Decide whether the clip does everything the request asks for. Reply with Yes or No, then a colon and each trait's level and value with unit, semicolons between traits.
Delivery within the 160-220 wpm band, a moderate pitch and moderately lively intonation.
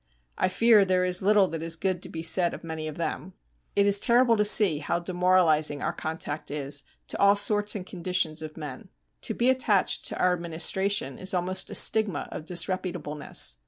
Yes: average, 195 wpm; medium, 180 Hz; average, 3.8 semitones